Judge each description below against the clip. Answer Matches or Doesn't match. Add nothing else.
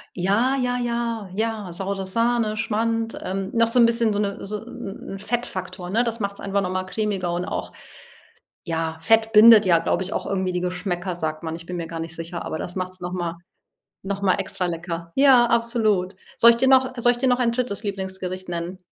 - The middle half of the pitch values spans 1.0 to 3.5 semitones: Doesn't match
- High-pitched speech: Matches